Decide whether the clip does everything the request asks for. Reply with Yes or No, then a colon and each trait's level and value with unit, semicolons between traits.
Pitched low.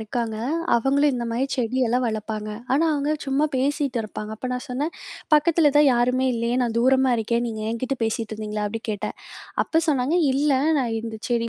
No: high, 245 Hz